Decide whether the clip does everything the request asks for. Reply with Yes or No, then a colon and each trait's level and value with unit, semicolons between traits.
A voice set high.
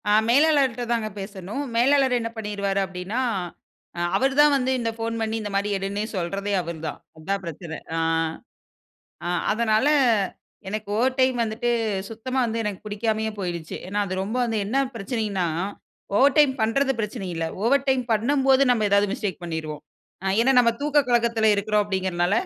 Yes: high, 220 Hz